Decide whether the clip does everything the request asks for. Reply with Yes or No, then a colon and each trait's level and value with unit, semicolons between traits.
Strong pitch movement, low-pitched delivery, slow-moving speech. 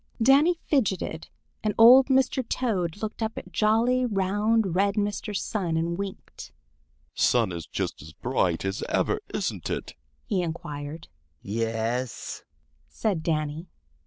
No: wide, 7.2 semitones; high, 190 Hz; slow, 130 wpm